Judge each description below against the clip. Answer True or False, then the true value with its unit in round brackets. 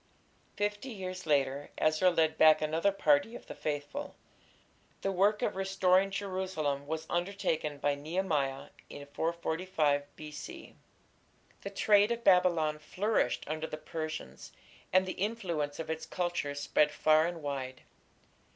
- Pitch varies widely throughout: False (4.0 semitones)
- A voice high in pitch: False (160 Hz)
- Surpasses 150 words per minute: False (135 wpm)